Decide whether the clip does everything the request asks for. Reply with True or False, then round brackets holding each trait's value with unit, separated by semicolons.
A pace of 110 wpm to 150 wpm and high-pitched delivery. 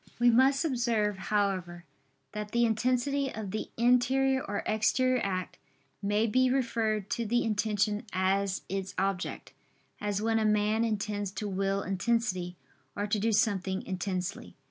True (145 wpm; 210 Hz)